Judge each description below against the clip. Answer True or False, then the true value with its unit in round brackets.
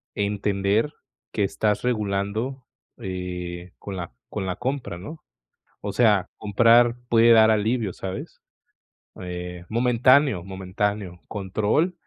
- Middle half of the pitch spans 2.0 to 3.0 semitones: False (3.8 semitones)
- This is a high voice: False (105 Hz)